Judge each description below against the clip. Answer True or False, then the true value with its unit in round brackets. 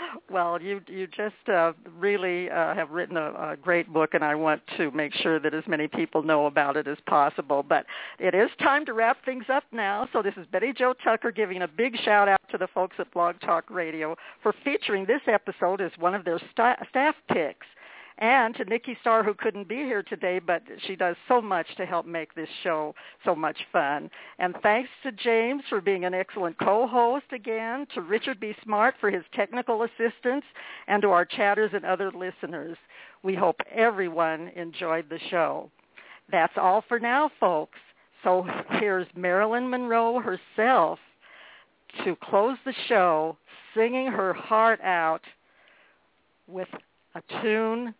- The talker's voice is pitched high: True (200 Hz)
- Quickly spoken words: False (175 wpm)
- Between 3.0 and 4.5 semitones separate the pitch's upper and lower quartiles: False (5.0 semitones)